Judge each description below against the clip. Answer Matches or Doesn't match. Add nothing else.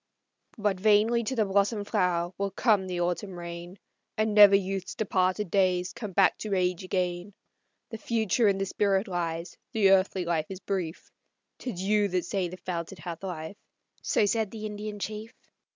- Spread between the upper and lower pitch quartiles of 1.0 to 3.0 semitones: Matches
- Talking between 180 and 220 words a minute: Doesn't match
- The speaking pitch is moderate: Doesn't match